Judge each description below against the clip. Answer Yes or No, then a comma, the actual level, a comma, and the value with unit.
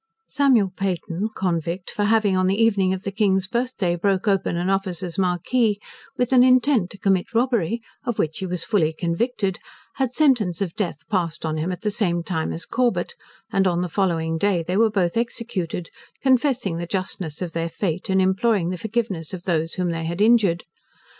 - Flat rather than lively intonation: No, average, 4.3 semitones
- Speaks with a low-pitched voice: No, high, 190 Hz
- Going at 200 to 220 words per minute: No, average, 190 wpm